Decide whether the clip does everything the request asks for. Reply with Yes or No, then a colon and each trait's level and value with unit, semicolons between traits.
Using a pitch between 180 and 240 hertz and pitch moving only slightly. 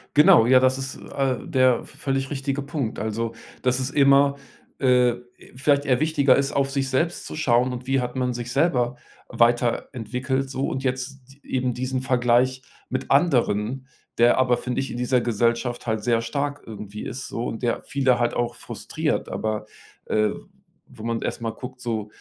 No: low, 125 Hz; narrow, 2.1 semitones